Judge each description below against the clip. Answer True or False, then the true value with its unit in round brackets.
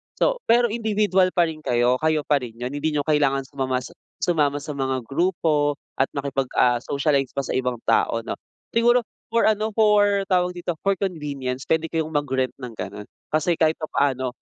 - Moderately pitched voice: True (150 Hz)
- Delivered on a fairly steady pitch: False (5.3 semitones)